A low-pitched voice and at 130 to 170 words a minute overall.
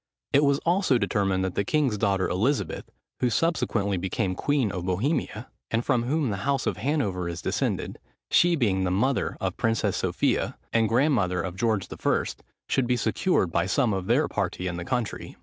No: low, 110 Hz; average, 185 wpm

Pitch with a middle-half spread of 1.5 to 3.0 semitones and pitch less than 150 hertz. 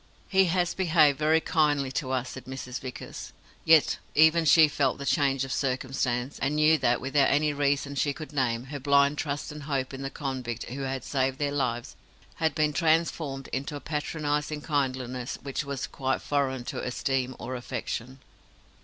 Yes: narrow, 2.4 semitones; medium, 140 Hz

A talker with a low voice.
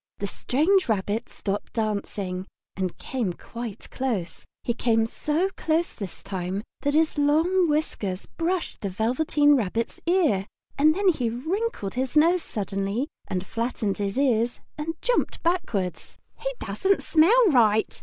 No: high, 245 Hz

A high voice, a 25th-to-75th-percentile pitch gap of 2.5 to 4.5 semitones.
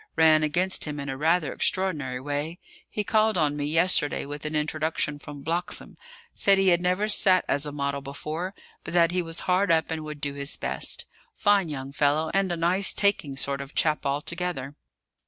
No: medium, 155 Hz; average, 3.8 semitones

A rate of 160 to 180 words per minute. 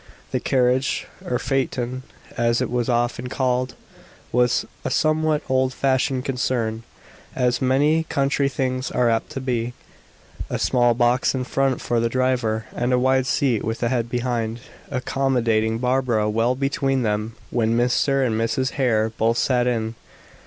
No: average, 150 wpm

